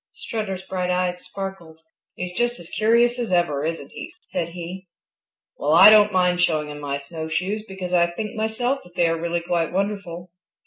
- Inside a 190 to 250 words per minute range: No, average, 180 wpm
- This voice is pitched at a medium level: Yes, medium, 180 Hz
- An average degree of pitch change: Yes, average, 3.7 semitones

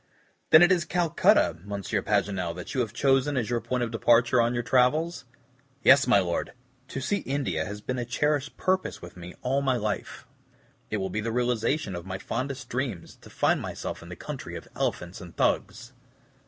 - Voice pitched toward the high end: No, low, 120 Hz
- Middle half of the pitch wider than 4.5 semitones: Yes, average, 5.2 semitones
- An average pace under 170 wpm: No, average, 195 wpm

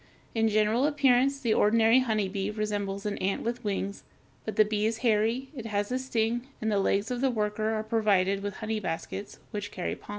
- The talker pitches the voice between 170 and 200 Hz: No, high, 215 Hz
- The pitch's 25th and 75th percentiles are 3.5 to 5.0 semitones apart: No, narrow, 2.4 semitones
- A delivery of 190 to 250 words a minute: Yes, average, 200 wpm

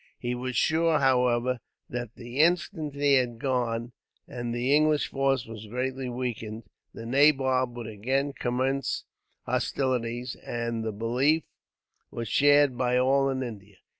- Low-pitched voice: Yes, low, 125 Hz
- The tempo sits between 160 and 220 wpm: No, slow, 135 wpm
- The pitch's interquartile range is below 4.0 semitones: Yes, narrow, 2.5 semitones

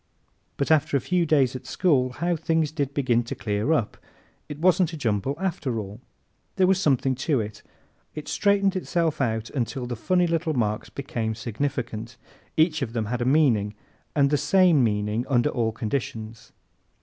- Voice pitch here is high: No, low, 135 Hz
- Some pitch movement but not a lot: No, wide, 5.7 semitones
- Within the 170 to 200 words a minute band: Yes, average, 175 wpm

